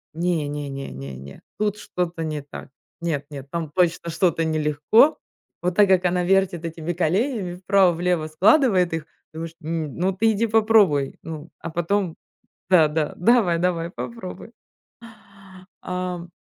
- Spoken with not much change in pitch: No, average, 3.2 semitones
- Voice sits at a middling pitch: Yes, medium, 175 Hz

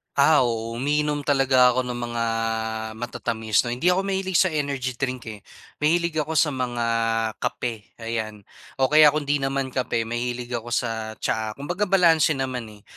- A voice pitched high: No, low, 130 Hz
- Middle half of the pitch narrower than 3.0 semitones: No, average, 4.2 semitones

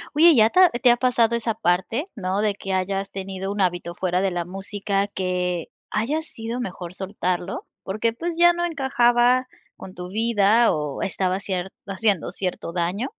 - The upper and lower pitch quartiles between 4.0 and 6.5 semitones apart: Yes, average, 4.4 semitones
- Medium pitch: No, high, 200 Hz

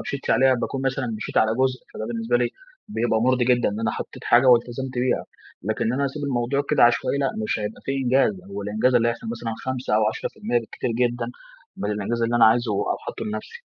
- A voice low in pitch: Yes, low, 120 Hz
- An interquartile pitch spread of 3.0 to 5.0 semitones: No, narrow, 2.5 semitones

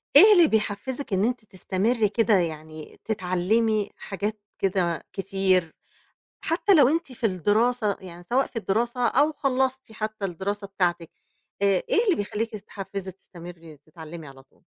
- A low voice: No, high, 205 Hz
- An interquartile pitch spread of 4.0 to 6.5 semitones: Yes, average, 4.7 semitones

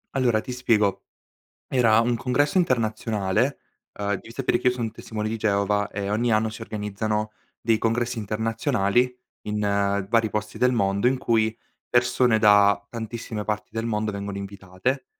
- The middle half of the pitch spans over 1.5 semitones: Yes, narrow, 2.6 semitones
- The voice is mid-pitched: No, low, 110 Hz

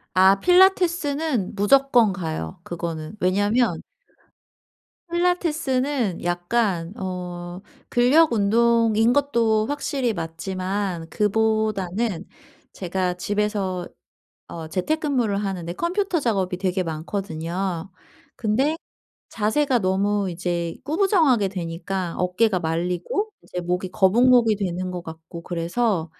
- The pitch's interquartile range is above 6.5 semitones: No, average, 5.3 semitones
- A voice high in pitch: Yes, high, 200 Hz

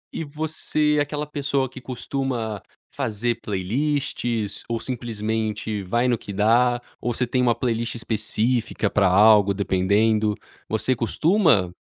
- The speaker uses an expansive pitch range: No, average, 3.6 semitones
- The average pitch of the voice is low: Yes, low, 115 Hz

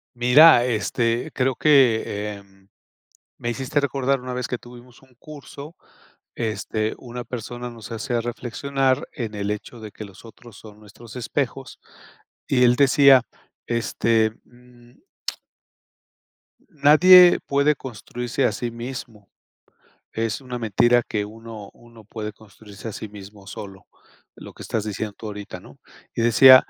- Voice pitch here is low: Yes, low, 120 Hz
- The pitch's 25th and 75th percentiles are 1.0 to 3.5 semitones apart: Yes, average, 3.1 semitones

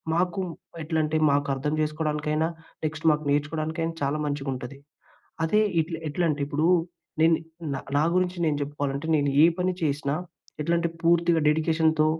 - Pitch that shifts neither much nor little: No, narrow, 2.0 semitones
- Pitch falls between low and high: Yes, medium, 155 Hz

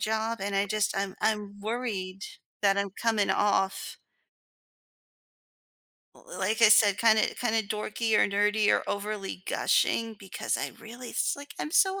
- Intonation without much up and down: Yes, narrow, 2.2 semitones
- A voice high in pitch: Yes, high, 215 Hz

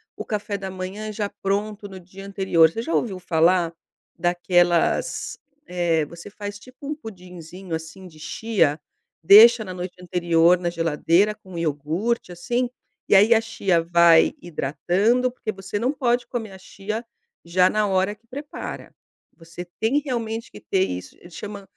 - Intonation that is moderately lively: Yes, average, 3.9 semitones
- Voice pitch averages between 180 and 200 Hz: Yes, high, 190 Hz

